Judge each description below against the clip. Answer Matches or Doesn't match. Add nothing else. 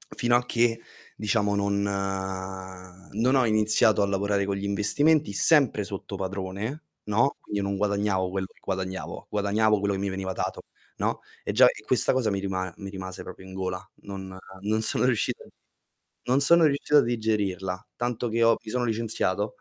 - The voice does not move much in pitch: Doesn't match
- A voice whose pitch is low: Matches